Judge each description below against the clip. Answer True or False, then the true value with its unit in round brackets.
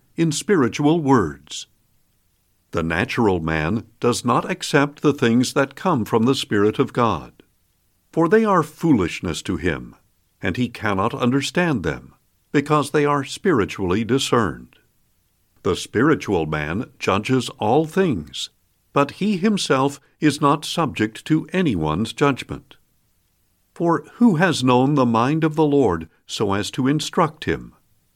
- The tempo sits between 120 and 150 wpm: True (135 wpm)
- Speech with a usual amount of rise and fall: False (7.7 semitones)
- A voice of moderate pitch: False (130 Hz)